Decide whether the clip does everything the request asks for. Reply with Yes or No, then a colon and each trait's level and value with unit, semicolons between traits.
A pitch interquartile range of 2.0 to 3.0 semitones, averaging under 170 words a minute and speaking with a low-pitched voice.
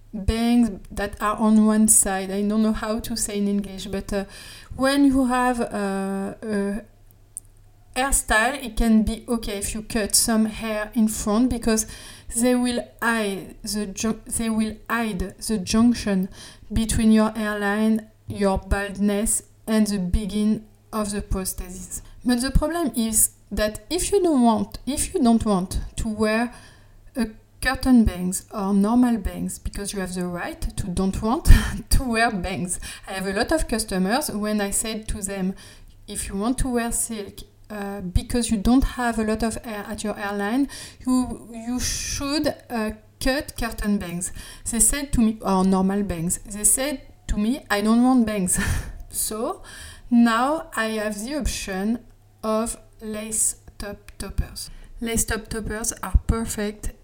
No: average, 2.7 semitones; average, 160 wpm; high, 215 Hz